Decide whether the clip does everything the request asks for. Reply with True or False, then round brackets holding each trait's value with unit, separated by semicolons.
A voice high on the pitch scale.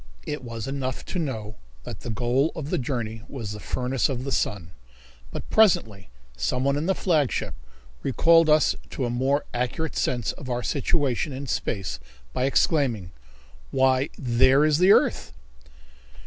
False (130 Hz)